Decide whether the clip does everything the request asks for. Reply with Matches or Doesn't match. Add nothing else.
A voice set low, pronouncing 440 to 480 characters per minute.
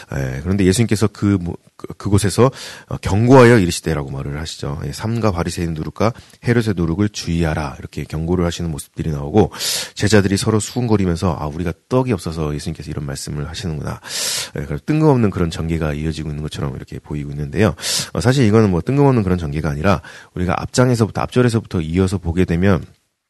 Matches